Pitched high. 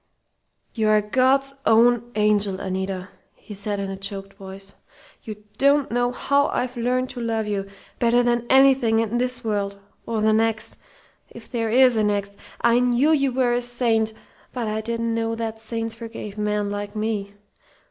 Yes: high, 225 Hz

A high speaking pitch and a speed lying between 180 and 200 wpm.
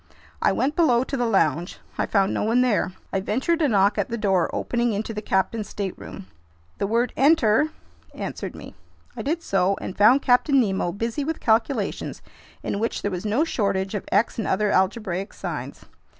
Yes: high, 215 Hz; average, 185 wpm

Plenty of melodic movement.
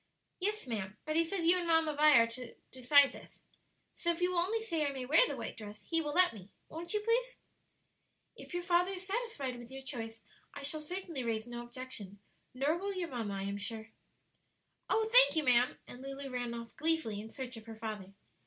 Yes: wide, 7.0 semitones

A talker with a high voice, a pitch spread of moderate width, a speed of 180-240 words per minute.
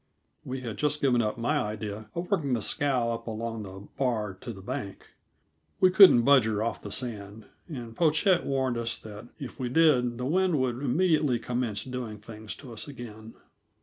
No: low, 120 Hz; average, 4.3 semitones; average, 185 wpm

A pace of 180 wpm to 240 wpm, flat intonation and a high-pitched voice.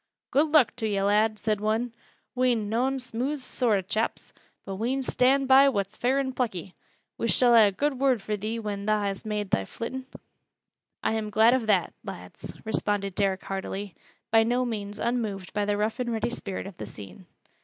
No: average, 190 wpm; average, 3.6 semitones; high, 220 Hz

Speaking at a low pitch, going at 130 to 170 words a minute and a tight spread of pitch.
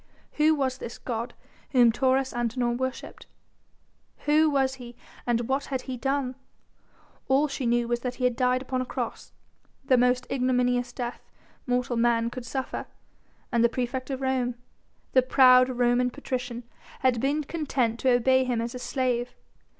No: very high, 250 Hz; average, 160 wpm; narrow, 1.5 semitones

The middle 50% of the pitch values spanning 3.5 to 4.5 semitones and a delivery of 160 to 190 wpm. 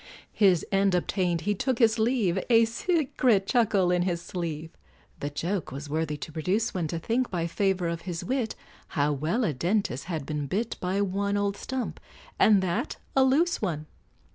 No: average, 4.9 semitones; average, 180 wpm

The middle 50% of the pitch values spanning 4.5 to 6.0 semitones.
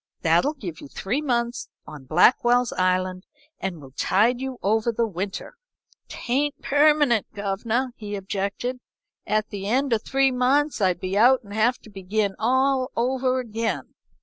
Yes: average, 4.8 semitones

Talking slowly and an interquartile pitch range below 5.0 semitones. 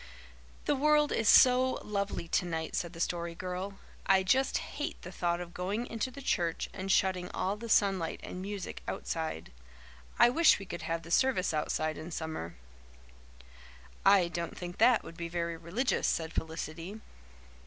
No: average, 165 wpm; average, 3.9 semitones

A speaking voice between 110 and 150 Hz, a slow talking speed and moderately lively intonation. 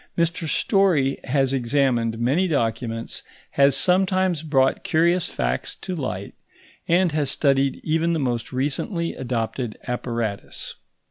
No: medium, 140 Hz; slow, 120 wpm; wide, 5.7 semitones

